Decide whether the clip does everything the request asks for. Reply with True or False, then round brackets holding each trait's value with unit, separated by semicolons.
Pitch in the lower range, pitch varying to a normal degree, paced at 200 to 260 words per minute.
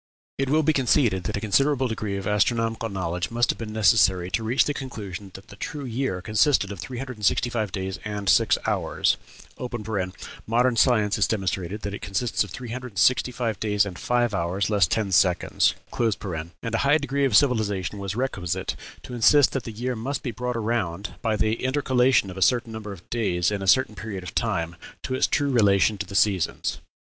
True (110 Hz; 4.1 semitones; 205 wpm)